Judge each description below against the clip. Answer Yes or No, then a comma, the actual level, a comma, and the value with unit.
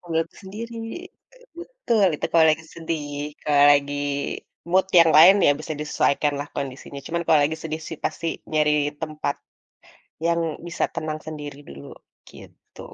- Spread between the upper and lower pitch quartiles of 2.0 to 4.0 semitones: Yes, narrow, 2.4 semitones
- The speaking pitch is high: No, medium, 160 Hz